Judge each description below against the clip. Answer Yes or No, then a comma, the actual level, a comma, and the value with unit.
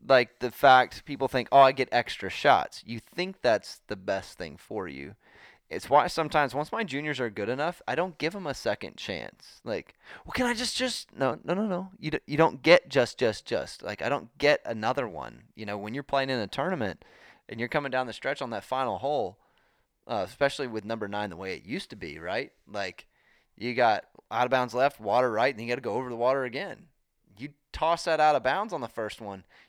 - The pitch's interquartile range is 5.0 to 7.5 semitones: Yes, wide, 5.4 semitones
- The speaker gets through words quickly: Yes, fast, 235 wpm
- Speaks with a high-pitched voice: No, low, 135 Hz